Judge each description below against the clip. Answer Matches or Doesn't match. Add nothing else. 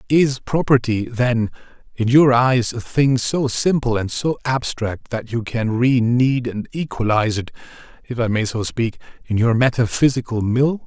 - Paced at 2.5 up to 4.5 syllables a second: Matches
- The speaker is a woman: Doesn't match